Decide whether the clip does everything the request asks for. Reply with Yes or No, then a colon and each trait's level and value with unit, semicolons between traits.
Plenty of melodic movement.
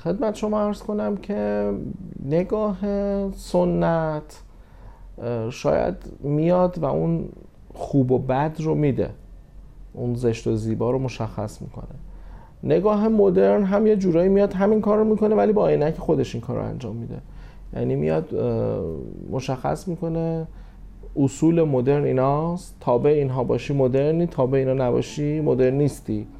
Yes: wide, 6.7 semitones